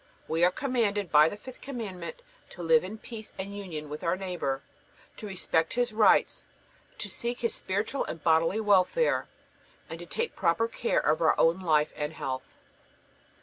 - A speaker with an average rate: Yes, average, 170 wpm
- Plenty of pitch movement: Yes, wide, 5.9 semitones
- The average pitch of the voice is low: No, high, 195 Hz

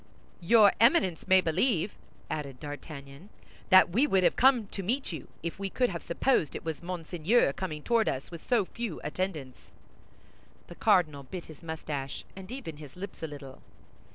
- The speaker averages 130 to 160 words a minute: No, average, 170 wpm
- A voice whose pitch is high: No, medium, 175 Hz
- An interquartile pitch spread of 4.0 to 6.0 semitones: Yes, average, 5.0 semitones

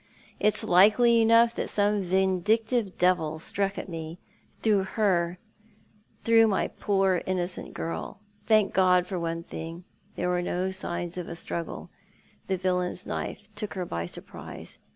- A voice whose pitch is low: No, medium, 185 Hz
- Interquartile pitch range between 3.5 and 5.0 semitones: No, average, 3.0 semitones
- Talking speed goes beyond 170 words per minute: No, average, 145 wpm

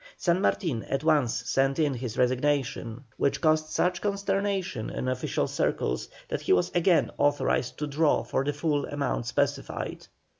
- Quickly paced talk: No, average, 155 wpm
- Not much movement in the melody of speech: No, average, 4.2 semitones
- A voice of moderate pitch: Yes, medium, 145 Hz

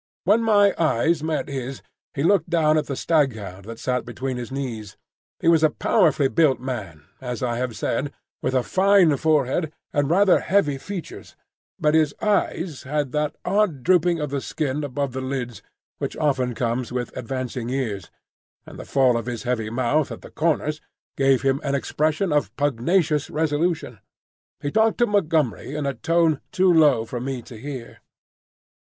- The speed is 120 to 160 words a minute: No, average, 170 wpm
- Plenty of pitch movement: No, average, 4.3 semitones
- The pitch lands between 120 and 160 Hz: Yes, medium, 140 Hz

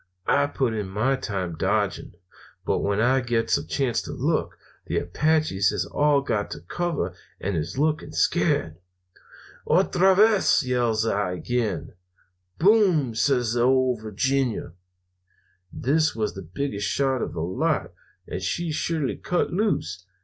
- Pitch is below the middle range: Yes, low, 125 Hz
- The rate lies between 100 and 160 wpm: Yes, average, 140 wpm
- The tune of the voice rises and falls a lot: Yes, wide, 6.7 semitones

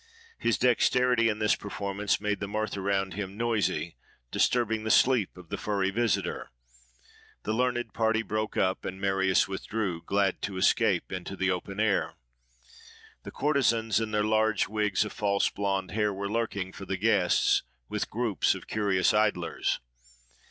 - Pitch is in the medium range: No, low, 105 Hz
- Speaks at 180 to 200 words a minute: No, average, 155 wpm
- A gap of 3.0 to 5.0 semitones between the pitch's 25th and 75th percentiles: No, narrow, 2.4 semitones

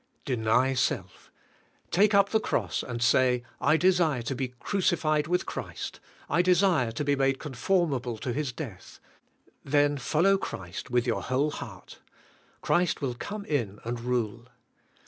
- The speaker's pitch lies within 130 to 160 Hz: Yes, low, 135 Hz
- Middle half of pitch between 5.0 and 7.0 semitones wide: Yes, wide, 5.6 semitones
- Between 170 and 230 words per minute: No, average, 145 wpm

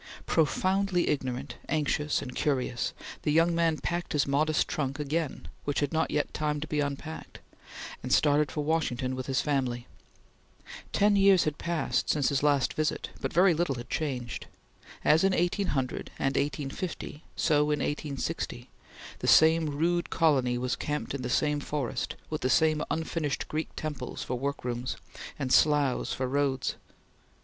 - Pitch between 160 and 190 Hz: No, medium, 150 Hz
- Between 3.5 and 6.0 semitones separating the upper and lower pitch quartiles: No, average, 3.0 semitones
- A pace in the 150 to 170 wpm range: Yes, average, 155 wpm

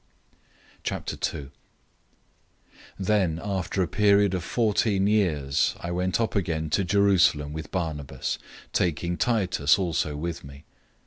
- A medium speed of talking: No, slow, 115 wpm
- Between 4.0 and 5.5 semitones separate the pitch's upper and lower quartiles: Yes, average, 4.4 semitones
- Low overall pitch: Yes, very low, 90 Hz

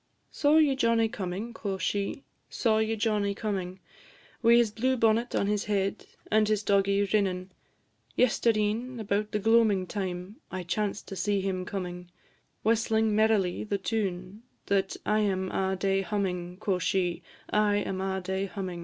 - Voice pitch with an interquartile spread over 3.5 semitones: No, narrow, 2.5 semitones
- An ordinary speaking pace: Yes, average, 155 wpm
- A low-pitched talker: No, high, 200 Hz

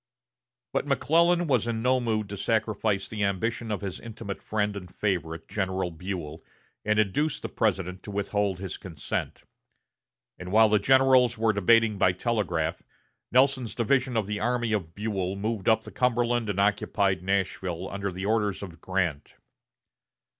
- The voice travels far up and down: No, average, 3.3 semitones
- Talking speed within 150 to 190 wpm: Yes, average, 155 wpm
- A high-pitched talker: No, low, 105 Hz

